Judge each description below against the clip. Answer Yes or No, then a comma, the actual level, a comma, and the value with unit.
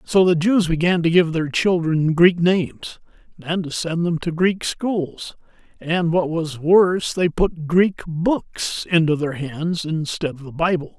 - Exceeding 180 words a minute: No, average, 175 wpm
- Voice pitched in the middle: Yes, medium, 170 Hz